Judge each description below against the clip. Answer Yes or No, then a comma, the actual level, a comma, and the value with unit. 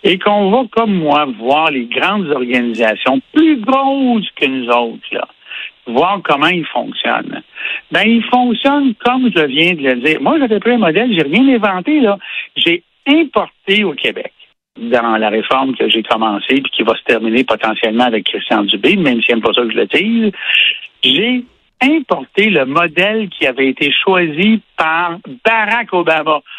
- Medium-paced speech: Yes, average, 170 wpm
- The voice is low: No, high, 195 Hz